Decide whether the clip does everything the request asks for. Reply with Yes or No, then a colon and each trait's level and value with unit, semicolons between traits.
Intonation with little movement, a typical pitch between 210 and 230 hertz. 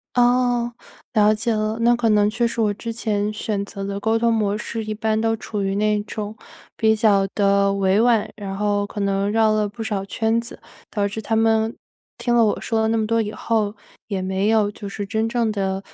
Yes: narrow, 1.8 semitones; high, 215 Hz